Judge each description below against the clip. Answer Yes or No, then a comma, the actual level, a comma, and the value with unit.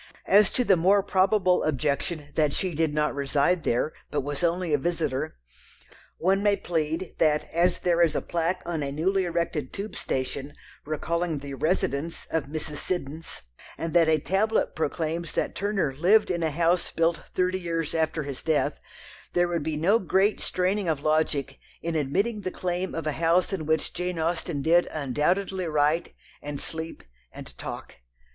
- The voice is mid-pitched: Yes, medium, 165 Hz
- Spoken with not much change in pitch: No, average, 3.1 semitones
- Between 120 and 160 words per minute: No, average, 170 wpm